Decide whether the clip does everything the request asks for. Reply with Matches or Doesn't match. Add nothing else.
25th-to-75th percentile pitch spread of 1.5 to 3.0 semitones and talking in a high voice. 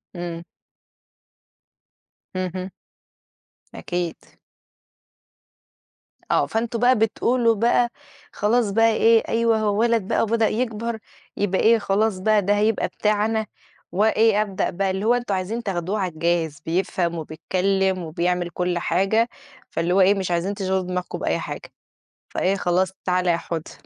Doesn't match